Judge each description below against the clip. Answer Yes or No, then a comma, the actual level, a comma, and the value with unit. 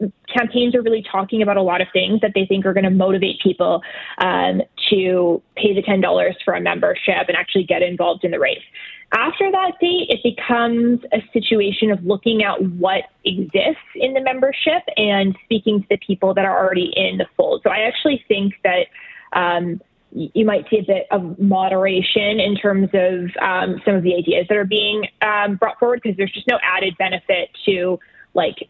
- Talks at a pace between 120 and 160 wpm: No, average, 195 wpm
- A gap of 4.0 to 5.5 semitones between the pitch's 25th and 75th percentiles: No, average, 3.2 semitones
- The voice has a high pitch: Yes, high, 200 Hz